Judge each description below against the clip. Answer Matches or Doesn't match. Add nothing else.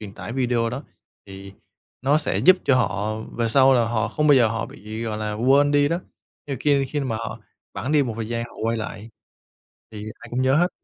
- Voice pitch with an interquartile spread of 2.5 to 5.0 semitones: Matches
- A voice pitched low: Matches